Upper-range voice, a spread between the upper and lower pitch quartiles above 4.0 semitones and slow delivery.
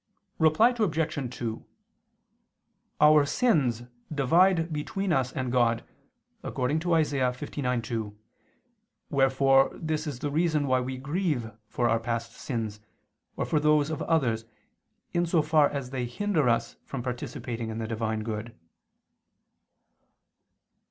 No: low, 135 Hz; average, 4.7 semitones; slow, 125 wpm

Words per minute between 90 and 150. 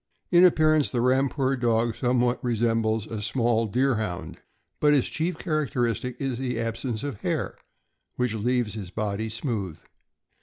Yes: average, 145 wpm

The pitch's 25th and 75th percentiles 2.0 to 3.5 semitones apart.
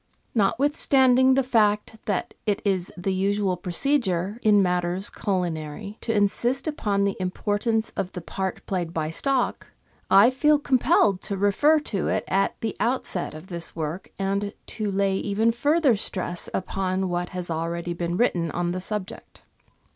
No: average, 4.1 semitones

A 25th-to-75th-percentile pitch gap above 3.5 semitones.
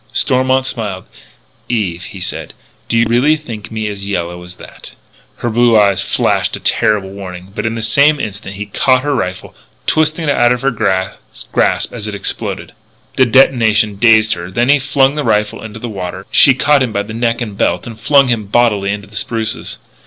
Yes: average, 3.9 semitones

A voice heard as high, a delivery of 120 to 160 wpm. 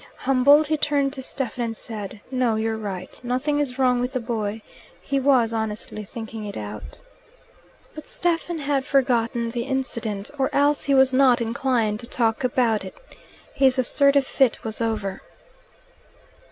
Yes: very high, 250 Hz; average, 155 wpm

